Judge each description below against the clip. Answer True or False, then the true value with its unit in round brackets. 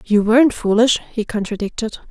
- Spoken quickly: False (145 wpm)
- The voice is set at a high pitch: True (225 Hz)